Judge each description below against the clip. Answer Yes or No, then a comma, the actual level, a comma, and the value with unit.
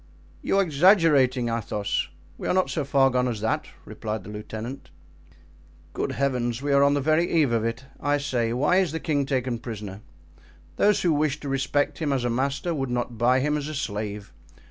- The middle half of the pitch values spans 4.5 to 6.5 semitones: No, average, 3.8 semitones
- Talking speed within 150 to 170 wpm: No, average, 200 wpm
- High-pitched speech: No, low, 135 Hz